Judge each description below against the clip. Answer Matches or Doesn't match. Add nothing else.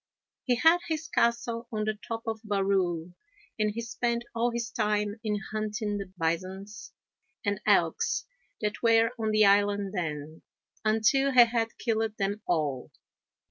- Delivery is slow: Doesn't match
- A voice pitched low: Doesn't match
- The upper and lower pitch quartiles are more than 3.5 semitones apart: Doesn't match